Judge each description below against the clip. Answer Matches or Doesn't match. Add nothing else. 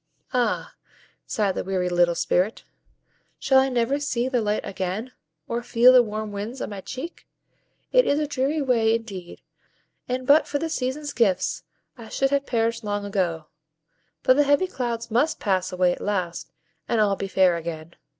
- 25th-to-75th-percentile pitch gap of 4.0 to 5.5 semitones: Matches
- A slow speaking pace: Doesn't match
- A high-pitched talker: Matches